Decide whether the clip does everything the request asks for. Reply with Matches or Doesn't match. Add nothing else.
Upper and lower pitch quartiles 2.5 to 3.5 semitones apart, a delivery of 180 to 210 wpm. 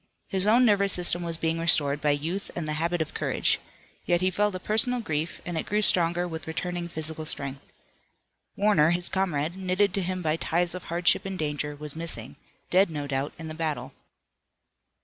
Matches